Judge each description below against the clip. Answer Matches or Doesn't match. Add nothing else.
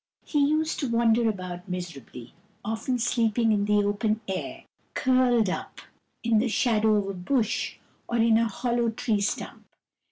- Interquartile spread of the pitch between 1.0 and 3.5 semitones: Matches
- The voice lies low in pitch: Doesn't match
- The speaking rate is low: Doesn't match